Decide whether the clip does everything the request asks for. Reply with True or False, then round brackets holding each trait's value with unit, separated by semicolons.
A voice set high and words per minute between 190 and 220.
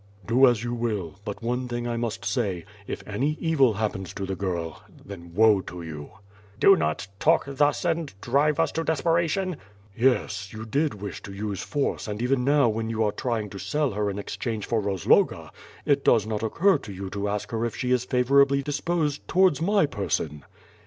False (115 Hz; 200 wpm)